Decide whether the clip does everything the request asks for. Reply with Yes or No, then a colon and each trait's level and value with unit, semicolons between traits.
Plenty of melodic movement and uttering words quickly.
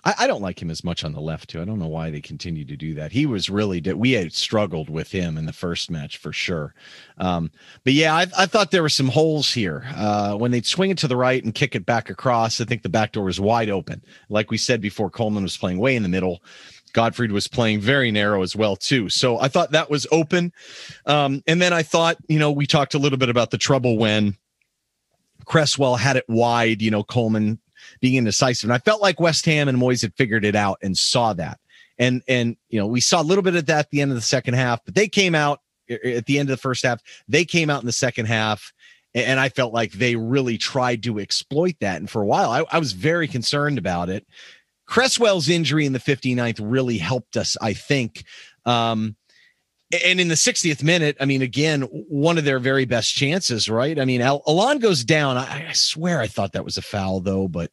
Yes: wide, 5.8 semitones; fast, 240 wpm